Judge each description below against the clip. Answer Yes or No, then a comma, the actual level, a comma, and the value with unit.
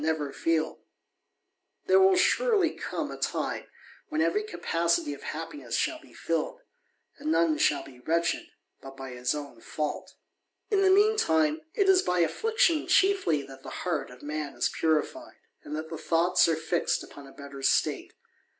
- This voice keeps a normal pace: Yes, average, 165 wpm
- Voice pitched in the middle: Yes, medium, 165 Hz